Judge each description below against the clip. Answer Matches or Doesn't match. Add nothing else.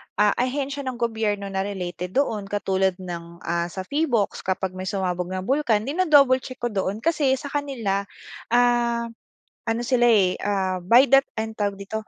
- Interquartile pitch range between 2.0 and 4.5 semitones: Doesn't match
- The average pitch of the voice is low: Doesn't match